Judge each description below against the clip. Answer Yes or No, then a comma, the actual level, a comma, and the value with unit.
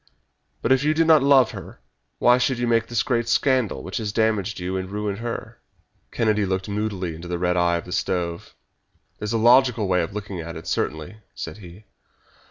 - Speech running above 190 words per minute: Yes, average, 200 wpm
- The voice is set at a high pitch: No, low, 105 Hz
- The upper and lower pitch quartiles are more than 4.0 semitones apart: Yes, average, 4.6 semitones